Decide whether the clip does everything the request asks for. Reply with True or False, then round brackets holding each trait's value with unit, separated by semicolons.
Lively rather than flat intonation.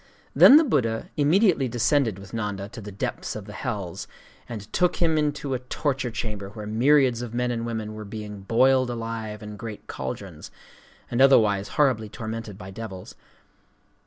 False (3.9 semitones)